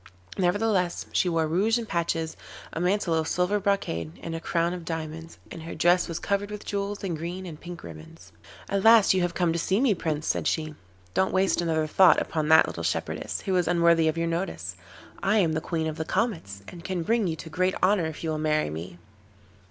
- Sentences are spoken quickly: Yes, fast, 220 wpm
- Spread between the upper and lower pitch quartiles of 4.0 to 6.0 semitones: No, average, 3.0 semitones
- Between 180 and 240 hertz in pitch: No, medium, 170 Hz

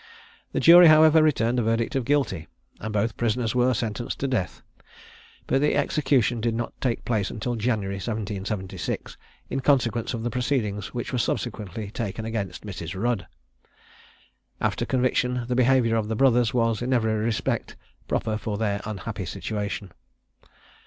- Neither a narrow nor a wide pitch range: Yes, average, 3.0 semitones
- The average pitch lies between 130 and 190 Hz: No, low, 115 Hz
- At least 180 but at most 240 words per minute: No, average, 150 wpm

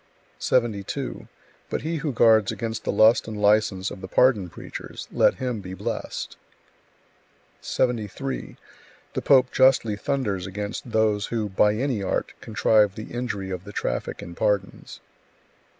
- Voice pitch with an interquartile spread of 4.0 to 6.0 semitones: No, average, 3.3 semitones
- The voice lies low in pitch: Yes, low, 110 Hz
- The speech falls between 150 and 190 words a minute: No, average, 140 wpm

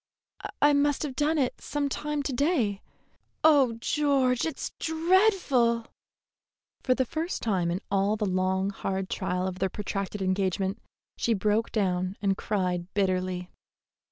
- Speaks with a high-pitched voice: Yes, high, 215 Hz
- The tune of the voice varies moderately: No, wide, 7.0 semitones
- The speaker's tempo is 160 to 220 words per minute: No, average, 140 wpm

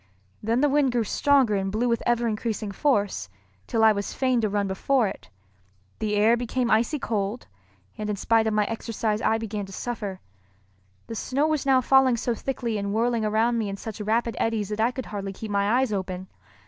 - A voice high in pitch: Yes, high, 225 Hz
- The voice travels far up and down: No, average, 2.7 semitones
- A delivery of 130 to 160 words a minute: No, fast, 205 wpm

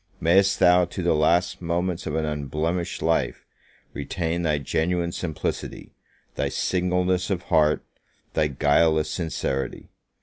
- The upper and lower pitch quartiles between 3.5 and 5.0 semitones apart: No, narrow, 2.6 semitones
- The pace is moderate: No, slow, 125 wpm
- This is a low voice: Yes, very low, 85 Hz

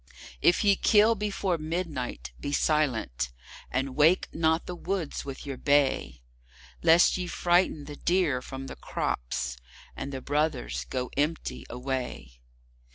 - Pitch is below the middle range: No, medium, 145 Hz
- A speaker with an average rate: No, slow, 130 wpm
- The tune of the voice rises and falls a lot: Yes, wide, 7.1 semitones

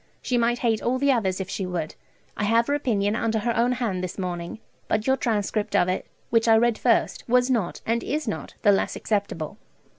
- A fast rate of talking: Yes, fast, 215 wpm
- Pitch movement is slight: No, average, 3.4 semitones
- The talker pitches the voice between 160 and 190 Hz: No, high, 225 Hz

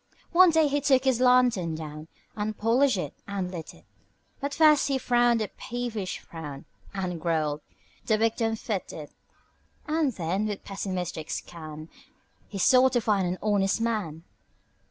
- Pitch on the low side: No, high, 210 Hz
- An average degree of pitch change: No, wide, 6.5 semitones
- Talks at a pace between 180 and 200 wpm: No, average, 155 wpm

